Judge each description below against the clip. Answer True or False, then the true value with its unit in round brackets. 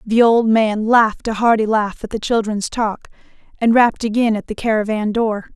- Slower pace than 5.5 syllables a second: True (5.2 syllables/s)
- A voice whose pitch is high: True (220 Hz)